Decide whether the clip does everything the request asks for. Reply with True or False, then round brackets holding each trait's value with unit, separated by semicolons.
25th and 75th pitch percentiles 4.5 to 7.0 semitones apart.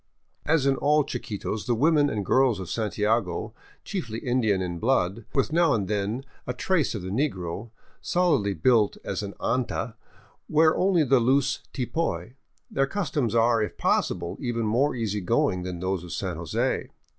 True (5.6 semitones)